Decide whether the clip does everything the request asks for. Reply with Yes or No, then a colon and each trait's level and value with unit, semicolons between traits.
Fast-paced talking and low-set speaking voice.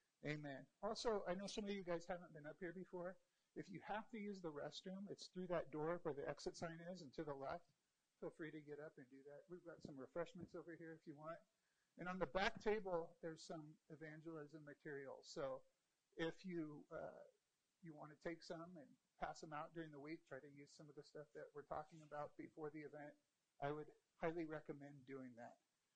No: fast, 220 wpm; medium, 165 Hz